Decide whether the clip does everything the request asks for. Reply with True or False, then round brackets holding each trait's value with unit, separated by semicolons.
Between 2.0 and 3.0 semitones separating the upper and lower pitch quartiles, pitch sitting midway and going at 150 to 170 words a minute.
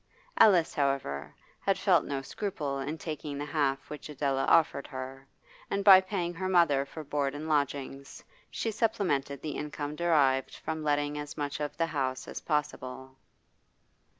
True (2.7 semitones; 145 Hz; 155 wpm)